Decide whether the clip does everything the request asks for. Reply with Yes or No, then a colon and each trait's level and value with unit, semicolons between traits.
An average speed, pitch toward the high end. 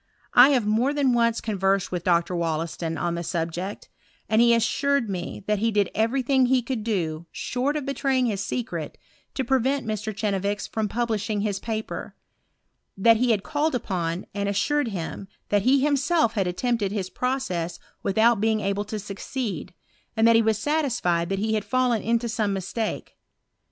Yes: average, 175 wpm; high, 220 Hz